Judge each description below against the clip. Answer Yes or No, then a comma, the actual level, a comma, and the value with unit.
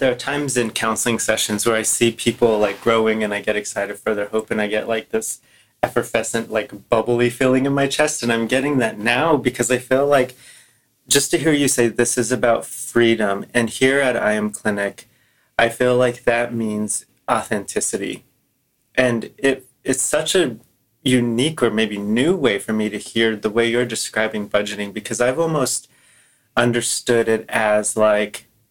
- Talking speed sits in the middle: Yes, average, 180 wpm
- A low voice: Yes, low, 115 Hz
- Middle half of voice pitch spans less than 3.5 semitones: Yes, average, 2.7 semitones